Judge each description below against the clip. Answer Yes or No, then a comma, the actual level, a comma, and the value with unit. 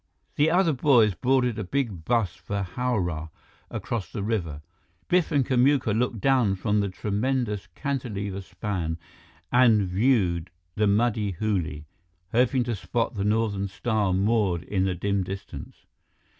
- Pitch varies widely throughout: No, average, 4.3 semitones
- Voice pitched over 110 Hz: No, low, 105 Hz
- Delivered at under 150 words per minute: Yes, average, 140 wpm